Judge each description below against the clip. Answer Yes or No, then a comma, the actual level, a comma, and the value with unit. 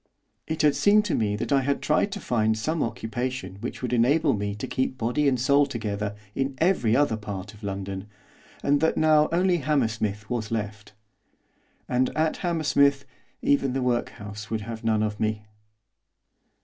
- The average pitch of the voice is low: Yes, low, 120 Hz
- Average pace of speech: Yes, average, 170 wpm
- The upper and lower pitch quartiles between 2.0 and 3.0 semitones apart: No, average, 5.0 semitones